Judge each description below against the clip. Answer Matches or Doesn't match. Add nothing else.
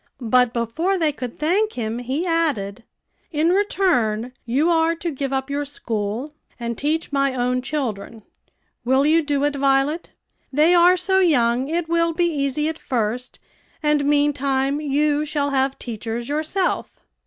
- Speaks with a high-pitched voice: Matches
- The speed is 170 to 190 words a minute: Doesn't match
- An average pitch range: Matches